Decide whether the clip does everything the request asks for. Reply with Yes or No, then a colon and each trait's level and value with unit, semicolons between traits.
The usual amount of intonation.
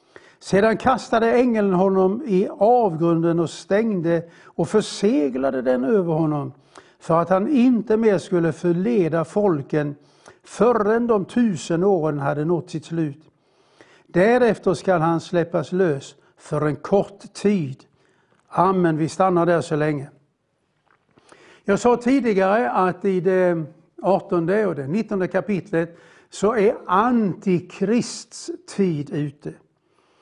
Yes: average, 4.4 semitones